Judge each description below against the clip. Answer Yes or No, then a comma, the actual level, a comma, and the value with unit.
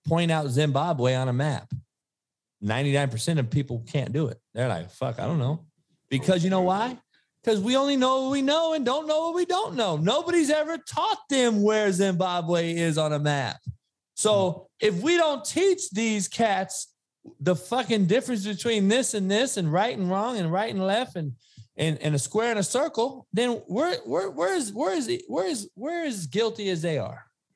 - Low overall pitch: No, high, 195 Hz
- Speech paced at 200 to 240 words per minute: Yes, fast, 205 wpm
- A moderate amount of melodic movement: No, wide, 8.5 semitones